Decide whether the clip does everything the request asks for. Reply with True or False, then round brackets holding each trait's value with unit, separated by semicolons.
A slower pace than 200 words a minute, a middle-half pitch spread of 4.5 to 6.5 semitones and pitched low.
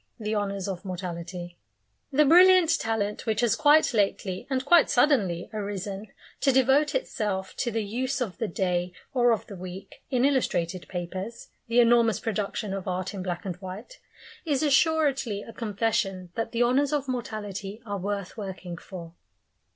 False (160 wpm; 5.1 semitones; 210 Hz)